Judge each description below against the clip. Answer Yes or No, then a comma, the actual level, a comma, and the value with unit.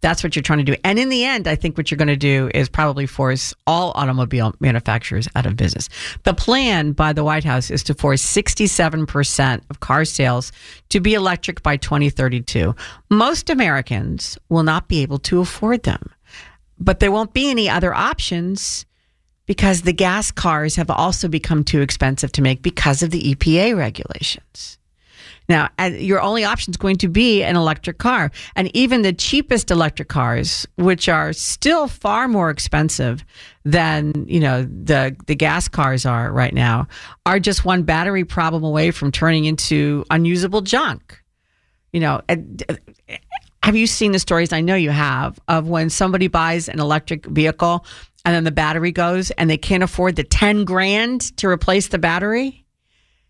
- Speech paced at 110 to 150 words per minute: No, average, 175 wpm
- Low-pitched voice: No, medium, 165 Hz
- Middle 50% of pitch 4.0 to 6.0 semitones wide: Yes, average, 4.8 semitones